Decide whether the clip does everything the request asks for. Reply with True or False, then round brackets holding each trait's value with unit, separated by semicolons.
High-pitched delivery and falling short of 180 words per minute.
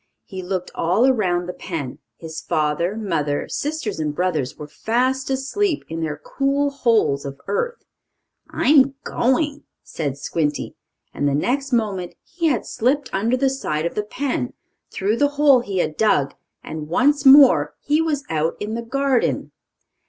True (215 Hz; 160 wpm)